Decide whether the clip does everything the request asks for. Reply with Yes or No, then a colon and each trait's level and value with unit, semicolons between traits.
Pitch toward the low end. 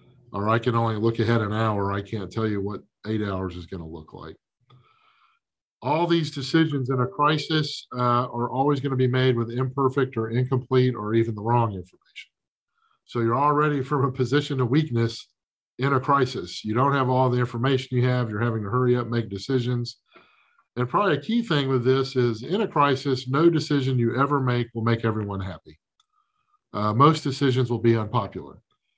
Yes: low, 125 Hz